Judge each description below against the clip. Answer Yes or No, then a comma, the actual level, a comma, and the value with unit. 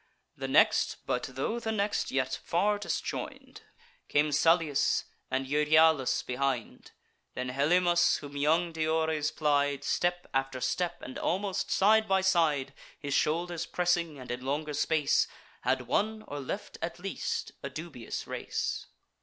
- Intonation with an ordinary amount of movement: Yes, average, 4.2 semitones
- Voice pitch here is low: No, medium, 155 Hz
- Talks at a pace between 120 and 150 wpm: Yes, slow, 135 wpm